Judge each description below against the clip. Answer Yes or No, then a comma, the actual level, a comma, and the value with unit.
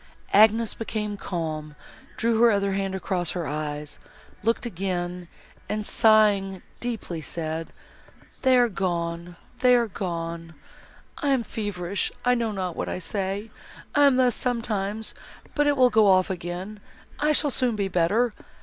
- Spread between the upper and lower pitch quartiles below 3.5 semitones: No, average, 4.7 semitones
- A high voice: Yes, high, 200 Hz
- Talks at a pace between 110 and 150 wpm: Yes, average, 145 wpm